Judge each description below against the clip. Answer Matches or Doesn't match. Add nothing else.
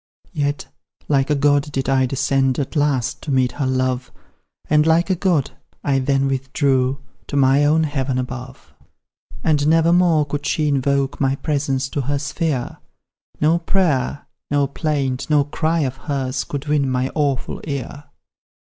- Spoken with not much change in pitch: Matches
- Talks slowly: Doesn't match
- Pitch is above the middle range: Doesn't match